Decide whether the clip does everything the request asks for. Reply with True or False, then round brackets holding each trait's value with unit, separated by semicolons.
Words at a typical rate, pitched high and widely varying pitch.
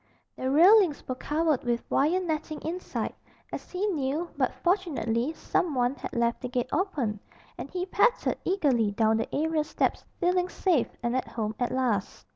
True (170 wpm; 295 Hz; 6.6 semitones)